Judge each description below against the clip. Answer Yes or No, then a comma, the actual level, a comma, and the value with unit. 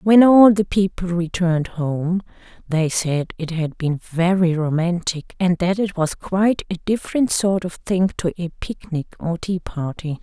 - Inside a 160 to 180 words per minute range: Yes, average, 175 wpm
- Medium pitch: Yes, medium, 175 Hz